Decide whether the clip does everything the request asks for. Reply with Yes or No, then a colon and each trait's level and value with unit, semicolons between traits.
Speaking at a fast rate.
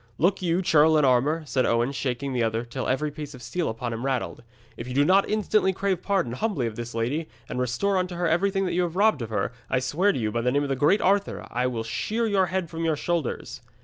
Yes: fast, 250 wpm